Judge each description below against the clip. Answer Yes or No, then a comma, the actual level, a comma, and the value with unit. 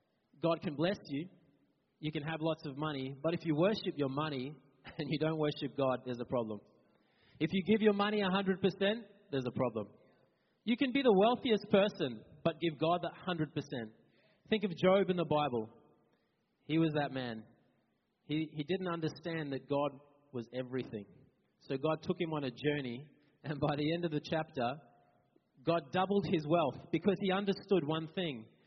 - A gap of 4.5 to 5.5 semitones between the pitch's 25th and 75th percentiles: Yes, average, 4.9 semitones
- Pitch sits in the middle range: Yes, medium, 155 Hz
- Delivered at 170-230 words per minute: Yes, average, 180 wpm